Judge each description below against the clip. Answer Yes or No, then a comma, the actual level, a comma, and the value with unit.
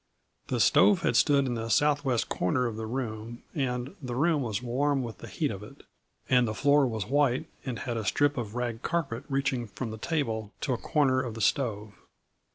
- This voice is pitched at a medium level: No, low, 125 Hz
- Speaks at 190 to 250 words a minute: Yes, fast, 205 wpm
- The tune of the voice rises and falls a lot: No, average, 3.8 semitones